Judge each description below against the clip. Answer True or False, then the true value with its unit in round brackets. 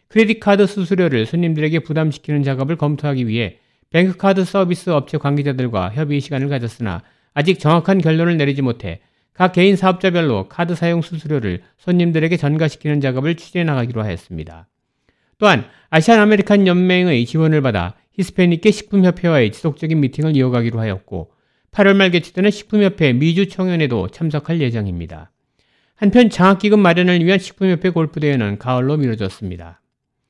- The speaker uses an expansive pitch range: True (6.7 semitones)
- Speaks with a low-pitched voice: False (155 Hz)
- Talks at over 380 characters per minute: True (400 characters per minute)